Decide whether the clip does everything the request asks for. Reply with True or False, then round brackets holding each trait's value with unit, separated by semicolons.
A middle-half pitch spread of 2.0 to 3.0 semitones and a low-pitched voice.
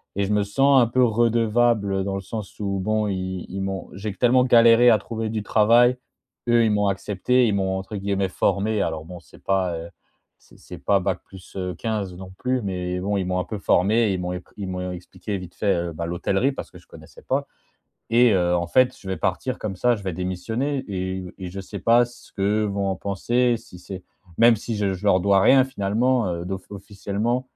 False (3.6 semitones; 100 Hz)